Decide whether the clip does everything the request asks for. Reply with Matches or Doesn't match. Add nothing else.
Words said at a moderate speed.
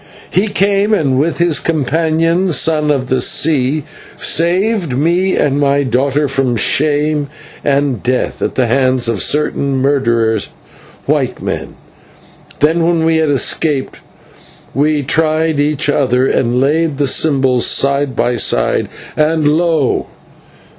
Doesn't match